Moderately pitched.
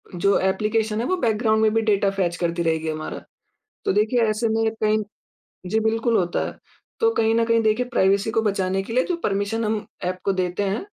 No: high, 215 Hz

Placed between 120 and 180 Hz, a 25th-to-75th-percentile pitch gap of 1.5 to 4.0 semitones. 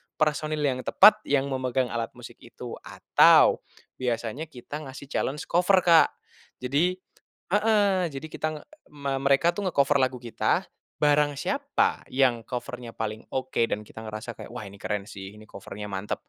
No: low, 135 Hz; average, 4.6 semitones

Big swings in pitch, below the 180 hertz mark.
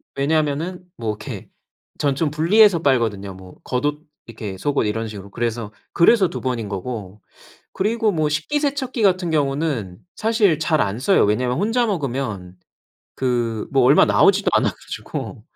Yes: wide, 7.9 semitones; medium, 140 Hz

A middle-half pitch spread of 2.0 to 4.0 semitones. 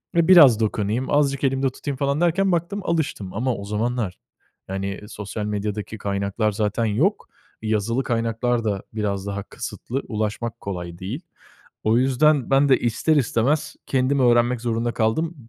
No: average, 4.6 semitones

